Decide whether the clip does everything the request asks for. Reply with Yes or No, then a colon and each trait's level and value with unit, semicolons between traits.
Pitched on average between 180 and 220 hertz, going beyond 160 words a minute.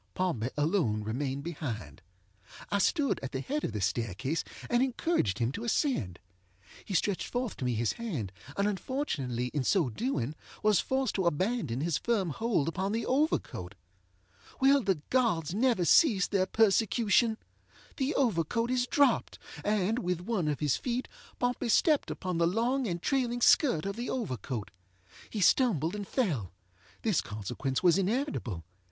No: high, 190 Hz; average, 155 wpm